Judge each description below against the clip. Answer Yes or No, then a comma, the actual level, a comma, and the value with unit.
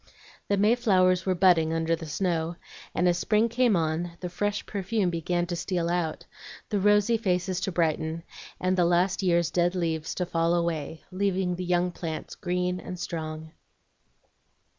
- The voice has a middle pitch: Yes, medium, 175 Hz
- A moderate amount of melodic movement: No, narrow, 2.1 semitones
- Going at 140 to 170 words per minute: Yes, average, 160 wpm